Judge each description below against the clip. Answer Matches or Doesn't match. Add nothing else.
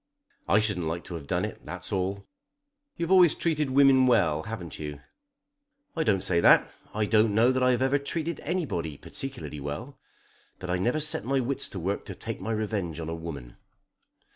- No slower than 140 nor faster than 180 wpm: Doesn't match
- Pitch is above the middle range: Doesn't match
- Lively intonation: Matches